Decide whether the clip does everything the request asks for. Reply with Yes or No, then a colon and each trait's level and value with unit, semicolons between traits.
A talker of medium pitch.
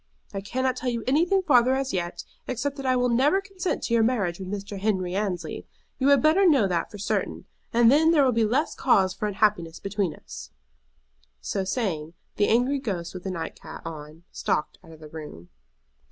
No: high, 215 Hz